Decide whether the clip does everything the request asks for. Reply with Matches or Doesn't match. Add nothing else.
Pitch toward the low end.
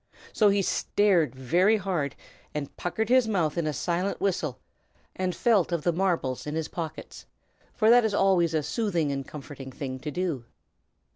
Doesn't match